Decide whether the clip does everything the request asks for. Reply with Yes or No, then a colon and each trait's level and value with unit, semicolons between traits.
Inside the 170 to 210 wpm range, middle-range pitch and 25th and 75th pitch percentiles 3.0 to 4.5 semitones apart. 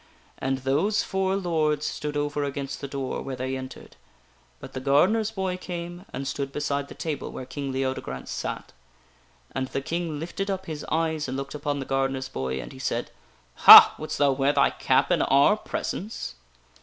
Yes: average, 180 wpm; medium, 145 Hz; average, 3.6 semitones